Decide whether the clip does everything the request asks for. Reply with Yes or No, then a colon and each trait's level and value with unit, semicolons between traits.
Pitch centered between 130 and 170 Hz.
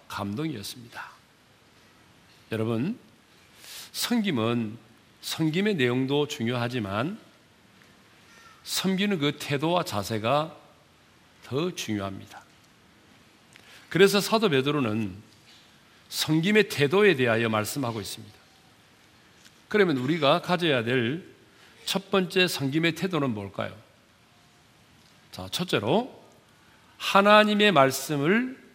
Yes: low, 135 Hz